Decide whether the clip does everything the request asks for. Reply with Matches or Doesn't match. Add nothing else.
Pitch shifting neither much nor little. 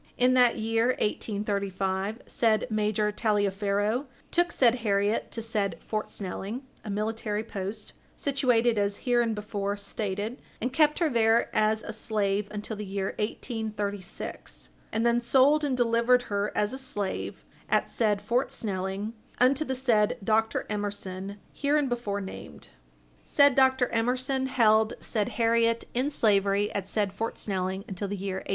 Matches